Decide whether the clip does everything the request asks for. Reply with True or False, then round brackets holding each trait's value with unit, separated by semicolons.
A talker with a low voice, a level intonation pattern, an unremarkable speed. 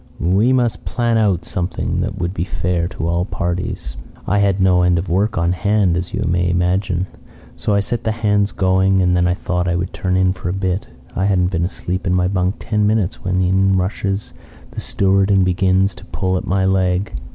False (95 Hz; 1.8 semitones; 210 wpm)